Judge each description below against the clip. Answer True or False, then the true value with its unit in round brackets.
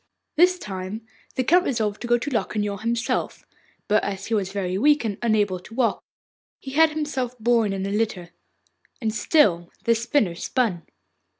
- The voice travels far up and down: False (4.2 semitones)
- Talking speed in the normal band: True (170 wpm)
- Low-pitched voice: False (225 Hz)